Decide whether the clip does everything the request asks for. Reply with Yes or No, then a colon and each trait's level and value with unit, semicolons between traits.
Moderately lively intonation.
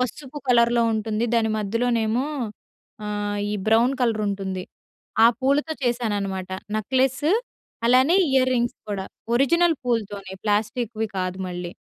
Yes: average, 3.7 semitones